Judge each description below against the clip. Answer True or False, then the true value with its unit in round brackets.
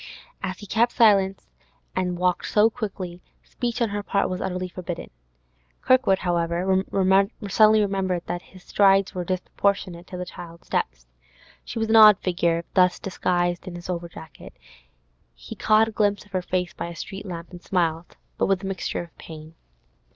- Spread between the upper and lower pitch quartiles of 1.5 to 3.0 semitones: True (2.4 semitones)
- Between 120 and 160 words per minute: False (175 wpm)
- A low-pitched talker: False (185 Hz)